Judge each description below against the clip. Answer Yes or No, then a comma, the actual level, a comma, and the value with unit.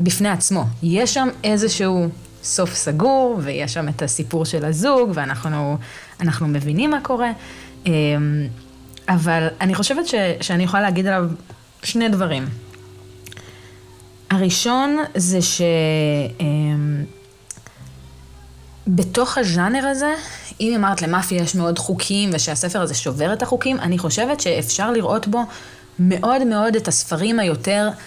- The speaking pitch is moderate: Yes, medium, 175 Hz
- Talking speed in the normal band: Yes, average, 115 wpm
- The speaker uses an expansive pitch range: Yes, wide, 6.2 semitones